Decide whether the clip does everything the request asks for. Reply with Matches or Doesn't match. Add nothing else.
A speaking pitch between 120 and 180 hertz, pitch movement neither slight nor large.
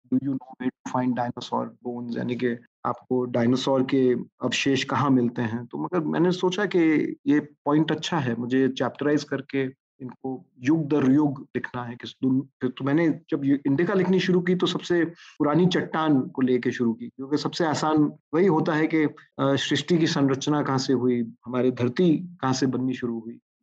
Matches